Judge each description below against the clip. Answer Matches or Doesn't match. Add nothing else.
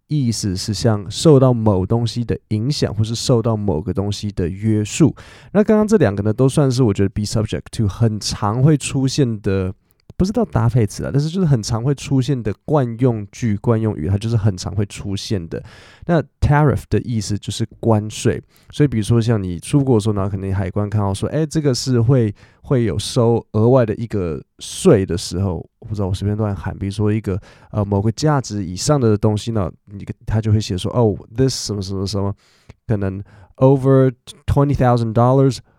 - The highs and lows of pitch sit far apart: Doesn't match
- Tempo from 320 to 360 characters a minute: Matches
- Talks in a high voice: Doesn't match